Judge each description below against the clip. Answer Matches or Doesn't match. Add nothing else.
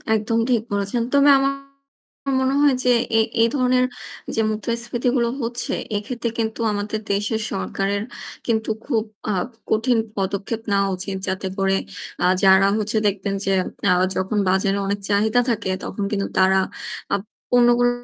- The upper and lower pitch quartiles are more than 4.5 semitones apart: Doesn't match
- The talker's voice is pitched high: Matches